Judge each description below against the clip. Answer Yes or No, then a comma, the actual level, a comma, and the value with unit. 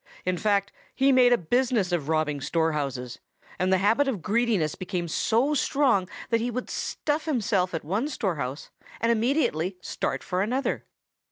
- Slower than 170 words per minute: Yes, average, 160 wpm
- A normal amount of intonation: No, wide, 6.5 semitones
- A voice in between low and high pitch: No, high, 200 Hz